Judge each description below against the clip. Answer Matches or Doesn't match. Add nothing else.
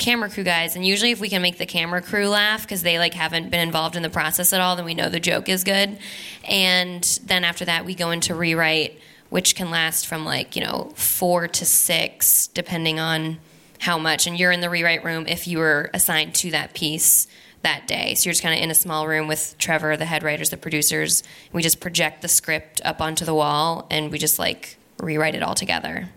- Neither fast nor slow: Doesn't match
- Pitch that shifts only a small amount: Matches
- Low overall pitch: Doesn't match